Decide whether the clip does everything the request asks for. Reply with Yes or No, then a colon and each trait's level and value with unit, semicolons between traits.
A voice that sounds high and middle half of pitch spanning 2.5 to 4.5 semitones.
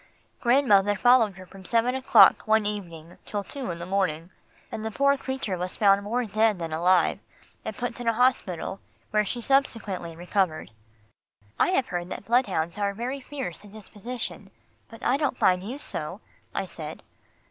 No: high, 210 Hz; average, 5.0 semitones